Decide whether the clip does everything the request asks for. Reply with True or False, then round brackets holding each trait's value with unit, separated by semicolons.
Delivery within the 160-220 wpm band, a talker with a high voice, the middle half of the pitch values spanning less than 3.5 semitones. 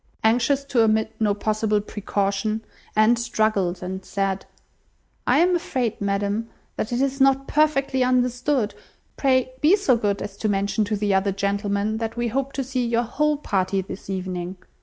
False (165 wpm; 220 Hz; 4.3 semitones)